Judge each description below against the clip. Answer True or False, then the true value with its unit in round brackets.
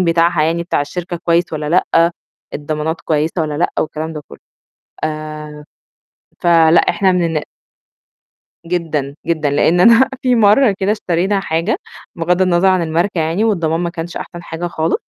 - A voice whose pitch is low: False (170 Hz)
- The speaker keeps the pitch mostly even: True (2.2 semitones)